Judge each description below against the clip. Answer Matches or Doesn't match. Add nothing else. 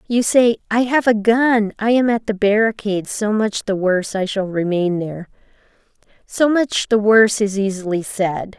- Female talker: Matches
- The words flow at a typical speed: Matches